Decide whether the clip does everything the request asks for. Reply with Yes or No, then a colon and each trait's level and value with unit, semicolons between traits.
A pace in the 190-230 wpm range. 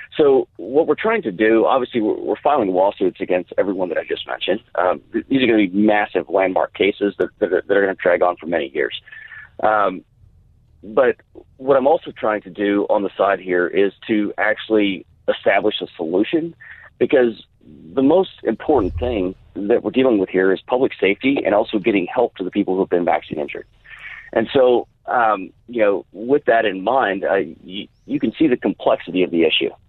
Yes: average, 200 wpm